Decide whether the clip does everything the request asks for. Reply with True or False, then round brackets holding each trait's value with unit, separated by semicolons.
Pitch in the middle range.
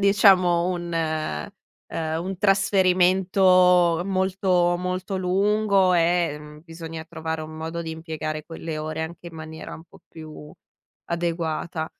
True (170 Hz)